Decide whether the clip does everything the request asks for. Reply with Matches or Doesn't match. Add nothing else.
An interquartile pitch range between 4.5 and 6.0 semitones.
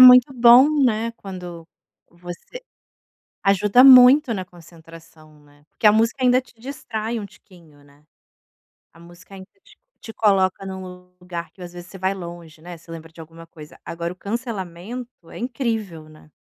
Matches